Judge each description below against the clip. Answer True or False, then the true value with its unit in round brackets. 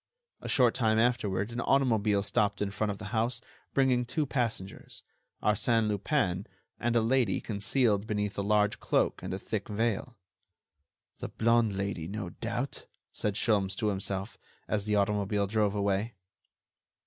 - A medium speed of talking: True (150 wpm)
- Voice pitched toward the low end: True (105 Hz)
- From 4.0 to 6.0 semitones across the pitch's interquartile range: False (2.7 semitones)